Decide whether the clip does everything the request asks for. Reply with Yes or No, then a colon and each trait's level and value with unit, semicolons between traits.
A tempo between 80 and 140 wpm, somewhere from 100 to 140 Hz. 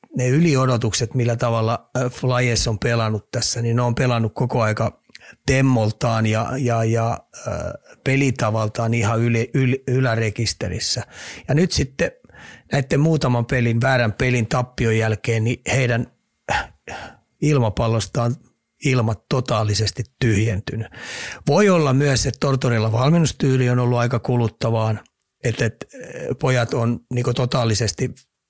Yes: average, 110 wpm; low, 120 Hz